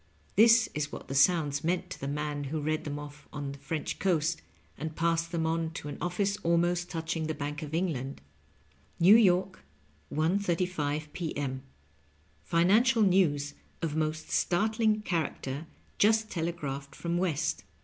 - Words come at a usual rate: Yes, average, 160 wpm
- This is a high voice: No, medium, 165 Hz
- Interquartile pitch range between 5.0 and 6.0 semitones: No, average, 3.7 semitones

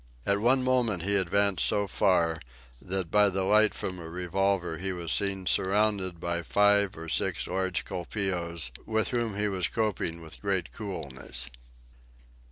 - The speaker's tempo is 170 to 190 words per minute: No, average, 155 wpm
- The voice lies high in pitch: No, very low, 95 Hz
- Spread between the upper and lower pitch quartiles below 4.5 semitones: Yes, average, 2.9 semitones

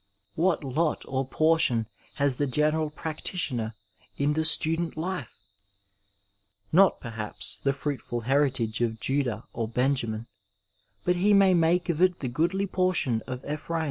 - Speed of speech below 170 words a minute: Yes, average, 140 wpm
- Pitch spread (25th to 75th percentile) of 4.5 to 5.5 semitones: Yes, average, 5.2 semitones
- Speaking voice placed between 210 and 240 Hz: No, medium, 145 Hz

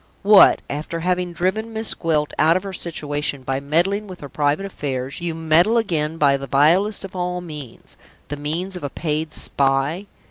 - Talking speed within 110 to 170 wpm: No, average, 180 wpm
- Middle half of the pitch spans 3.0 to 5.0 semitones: Yes, average, 3.9 semitones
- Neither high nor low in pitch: Yes, medium, 165 Hz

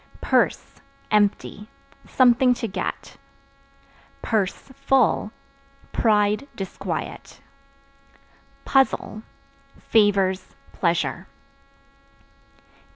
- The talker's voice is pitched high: Yes, high, 210 Hz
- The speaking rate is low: Yes, slow, 50 wpm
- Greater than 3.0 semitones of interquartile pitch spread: Yes, average, 3.8 semitones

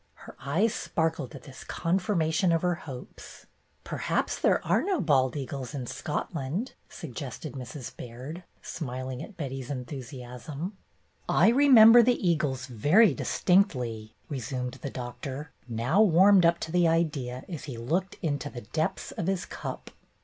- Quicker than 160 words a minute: No, average, 150 wpm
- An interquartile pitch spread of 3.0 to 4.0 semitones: No, wide, 5.6 semitones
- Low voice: No, medium, 150 Hz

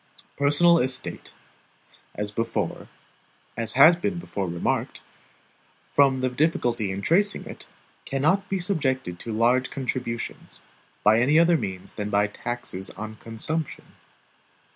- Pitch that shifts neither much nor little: No, wide, 6.4 semitones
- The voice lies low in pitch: Yes, low, 125 Hz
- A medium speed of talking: No, slow, 115 wpm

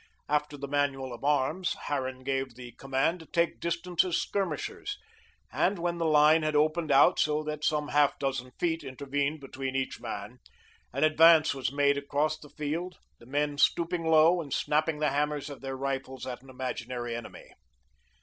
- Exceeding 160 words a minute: Yes, average, 175 wpm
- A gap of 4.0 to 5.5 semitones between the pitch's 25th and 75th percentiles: No, average, 2.9 semitones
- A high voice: No, medium, 145 Hz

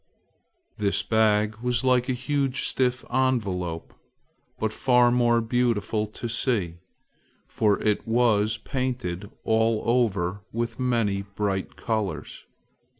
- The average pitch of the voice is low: Yes, low, 115 Hz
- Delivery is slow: Yes, slow, 110 wpm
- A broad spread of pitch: No, average, 3.1 semitones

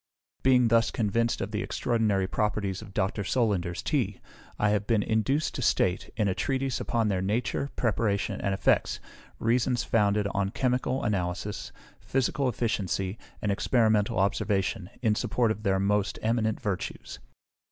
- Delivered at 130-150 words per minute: Yes, average, 145 wpm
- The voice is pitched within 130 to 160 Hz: No, low, 105 Hz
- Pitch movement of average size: Yes, average, 3.0 semitones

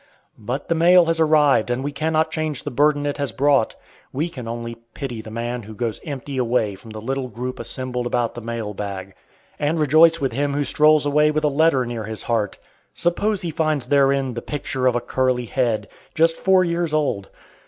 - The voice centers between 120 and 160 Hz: Yes, low, 135 Hz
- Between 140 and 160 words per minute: No, fast, 205 wpm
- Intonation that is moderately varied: Yes, average, 4.5 semitones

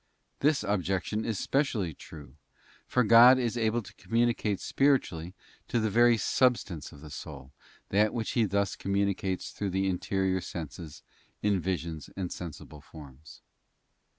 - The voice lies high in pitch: No, low, 100 Hz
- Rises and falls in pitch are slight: No, average, 5.2 semitones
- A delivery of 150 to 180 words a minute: No, average, 140 wpm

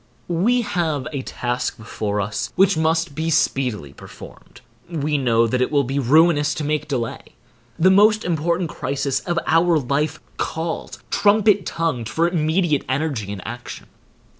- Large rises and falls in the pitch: No, average, 4.8 semitones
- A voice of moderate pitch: Yes, medium, 150 Hz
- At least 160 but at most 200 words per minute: No, average, 150 wpm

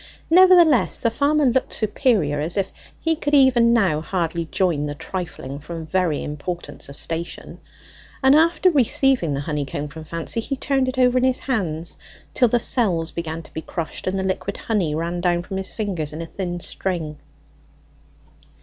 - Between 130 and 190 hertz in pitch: Yes, medium, 185 Hz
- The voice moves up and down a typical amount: No, wide, 7.7 semitones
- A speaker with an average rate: Yes, average, 175 wpm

